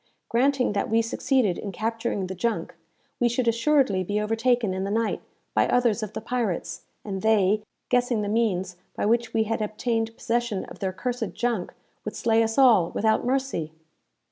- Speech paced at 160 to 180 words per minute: Yes, average, 175 wpm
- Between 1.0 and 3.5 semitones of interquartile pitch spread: Yes, average, 2.8 semitones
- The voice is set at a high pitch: Yes, high, 225 Hz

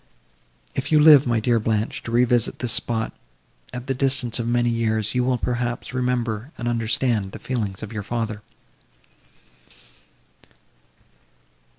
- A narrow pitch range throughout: Yes, narrow, 2.0 semitones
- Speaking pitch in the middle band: No, low, 120 Hz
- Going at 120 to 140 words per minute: Yes, slow, 135 wpm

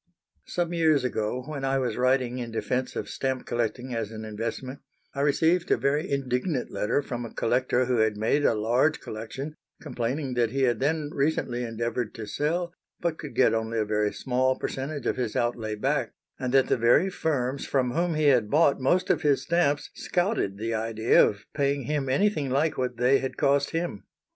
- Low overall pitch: Yes, low, 130 Hz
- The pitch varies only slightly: No, average, 3.9 semitones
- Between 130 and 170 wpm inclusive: No, average, 190 wpm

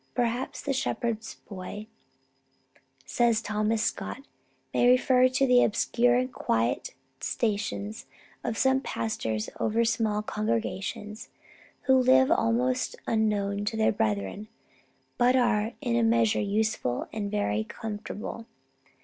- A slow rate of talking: Yes, slow, 115 wpm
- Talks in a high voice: Yes, high, 225 Hz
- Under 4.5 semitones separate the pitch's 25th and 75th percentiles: Yes, average, 2.8 semitones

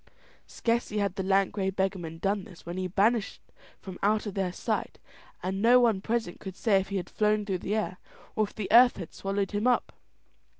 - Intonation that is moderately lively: No, narrow, 2.2 semitones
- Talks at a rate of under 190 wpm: No, fast, 205 wpm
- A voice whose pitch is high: Yes, high, 200 Hz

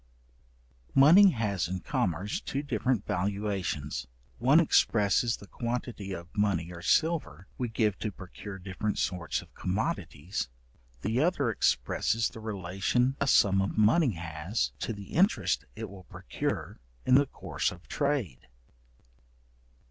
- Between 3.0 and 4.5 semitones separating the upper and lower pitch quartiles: No, average, 5.0 semitones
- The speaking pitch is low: Yes, low, 105 Hz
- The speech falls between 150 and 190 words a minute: No, slow, 135 wpm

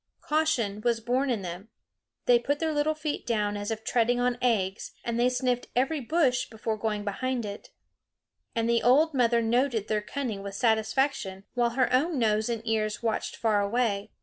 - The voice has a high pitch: Yes, high, 235 Hz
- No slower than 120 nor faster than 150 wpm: No, average, 180 wpm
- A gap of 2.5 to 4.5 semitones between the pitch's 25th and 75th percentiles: Yes, average, 3.1 semitones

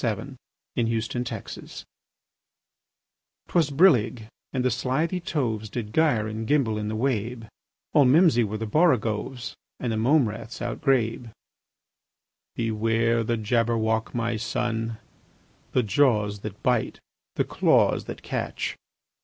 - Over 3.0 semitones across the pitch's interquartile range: No, average, 2.7 semitones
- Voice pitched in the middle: No, low, 115 Hz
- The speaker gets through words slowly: Yes, slow, 120 wpm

